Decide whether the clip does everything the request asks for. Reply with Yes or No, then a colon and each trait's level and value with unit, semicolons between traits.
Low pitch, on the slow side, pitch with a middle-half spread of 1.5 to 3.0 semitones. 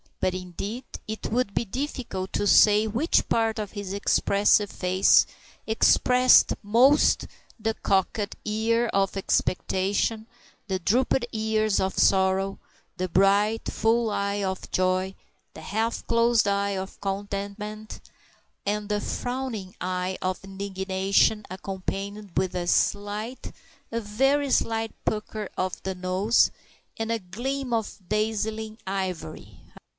No: high, 205 Hz; slow, 125 wpm; average, 2.7 semitones